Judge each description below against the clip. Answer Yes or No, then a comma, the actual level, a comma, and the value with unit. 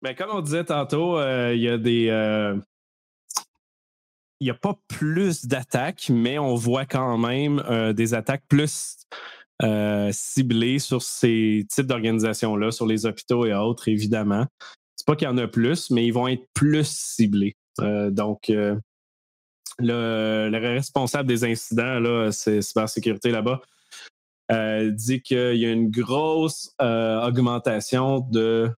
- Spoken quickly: No, average, 150 wpm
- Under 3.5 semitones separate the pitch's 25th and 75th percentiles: Yes, average, 3.1 semitones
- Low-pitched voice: Yes, low, 120 Hz